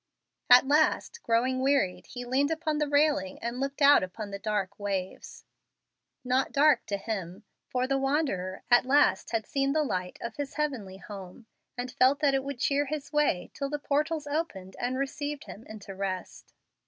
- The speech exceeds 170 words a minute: Yes, average, 180 wpm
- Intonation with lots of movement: Yes, wide, 6.1 semitones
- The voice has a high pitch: Yes, very high, 260 Hz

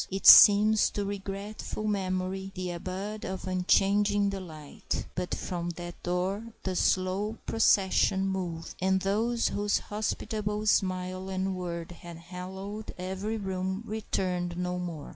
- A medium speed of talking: No, slow, 125 wpm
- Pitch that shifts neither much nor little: No, narrow, 2.1 semitones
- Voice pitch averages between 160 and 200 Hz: Yes, high, 190 Hz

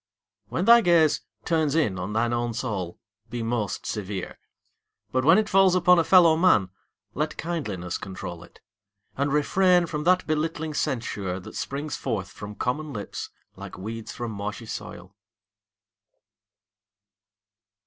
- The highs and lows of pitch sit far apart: Yes, wide, 7.8 semitones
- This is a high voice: No, low, 125 Hz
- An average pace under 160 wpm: Yes, average, 140 wpm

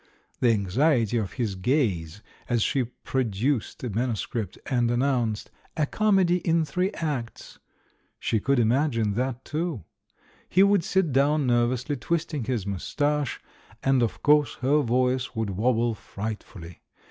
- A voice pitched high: No, low, 125 Hz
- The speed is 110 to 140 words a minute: Yes, slow, 135 wpm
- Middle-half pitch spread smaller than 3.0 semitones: No, average, 4.7 semitones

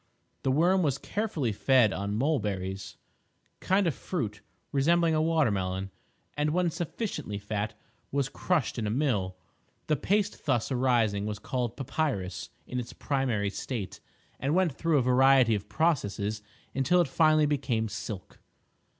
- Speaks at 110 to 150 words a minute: Yes, average, 140 wpm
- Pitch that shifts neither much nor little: No, wide, 7.0 semitones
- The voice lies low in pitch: Yes, low, 130 Hz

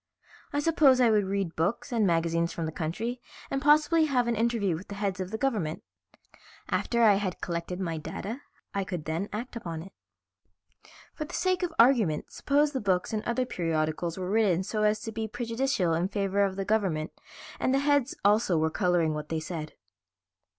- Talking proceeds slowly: No, average, 190 wpm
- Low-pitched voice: No, high, 200 Hz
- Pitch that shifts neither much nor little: No, wide, 5.9 semitones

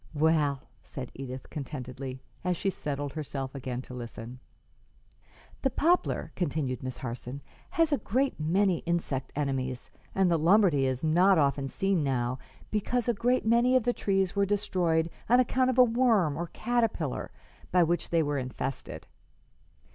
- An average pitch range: No, wide, 7.3 semitones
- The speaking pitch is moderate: Yes, medium, 160 Hz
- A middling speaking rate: Yes, average, 155 wpm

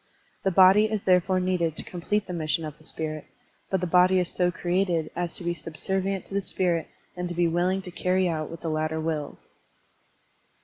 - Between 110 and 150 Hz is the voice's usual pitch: No, medium, 175 Hz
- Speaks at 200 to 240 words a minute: Yes, fast, 205 wpm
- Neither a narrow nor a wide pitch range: No, narrow, 2.3 semitones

